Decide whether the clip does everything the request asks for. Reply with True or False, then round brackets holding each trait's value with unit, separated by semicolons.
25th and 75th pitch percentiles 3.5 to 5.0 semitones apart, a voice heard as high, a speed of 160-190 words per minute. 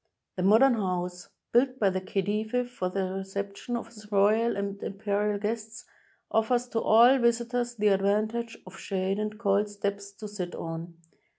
False (2.9 semitones; 210 Hz; 165 wpm)